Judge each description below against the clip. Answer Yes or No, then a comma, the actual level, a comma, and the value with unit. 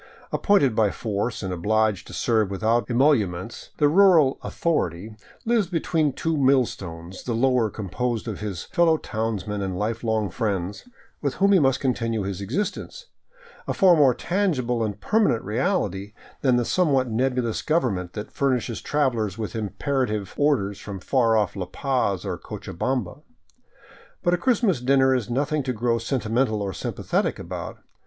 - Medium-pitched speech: No, low, 120 Hz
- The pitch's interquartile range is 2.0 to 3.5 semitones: No, average, 5.1 semitones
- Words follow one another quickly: No, average, 160 wpm